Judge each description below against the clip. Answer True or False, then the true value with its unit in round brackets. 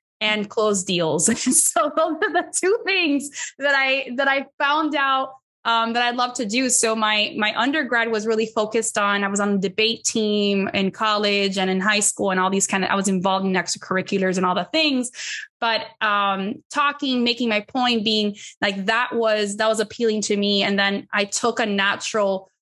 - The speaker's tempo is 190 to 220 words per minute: True (200 wpm)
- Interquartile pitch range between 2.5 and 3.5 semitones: False (4.4 semitones)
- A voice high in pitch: True (220 Hz)